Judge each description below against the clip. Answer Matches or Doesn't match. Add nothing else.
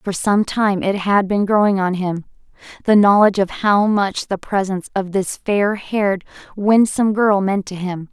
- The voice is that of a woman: Matches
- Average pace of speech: Matches